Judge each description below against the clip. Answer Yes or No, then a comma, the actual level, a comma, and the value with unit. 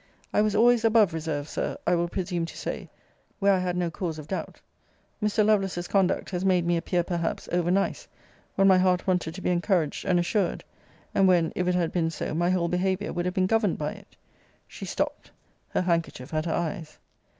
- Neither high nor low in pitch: Yes, medium, 180 Hz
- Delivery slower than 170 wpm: No, fast, 205 wpm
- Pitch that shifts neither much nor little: No, narrow, 2.2 semitones